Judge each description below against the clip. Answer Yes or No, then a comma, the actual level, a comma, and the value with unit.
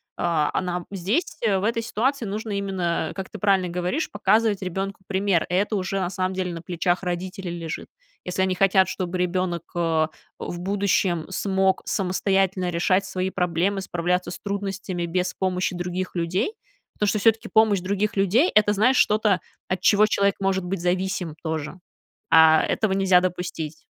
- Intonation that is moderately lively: No, narrow, 2.0 semitones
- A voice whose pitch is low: No, high, 190 Hz